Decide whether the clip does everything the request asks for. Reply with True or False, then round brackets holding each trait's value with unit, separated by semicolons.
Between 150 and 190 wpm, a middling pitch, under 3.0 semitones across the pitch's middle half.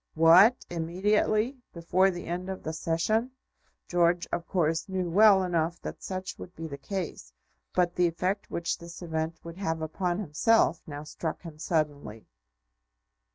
True (155 wpm; 170 Hz; 2.6 semitones)